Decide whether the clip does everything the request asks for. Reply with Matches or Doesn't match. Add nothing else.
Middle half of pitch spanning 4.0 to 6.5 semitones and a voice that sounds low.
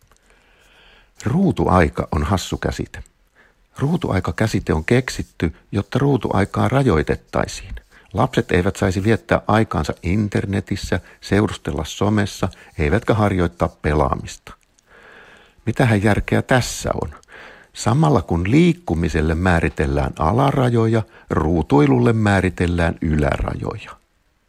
Matches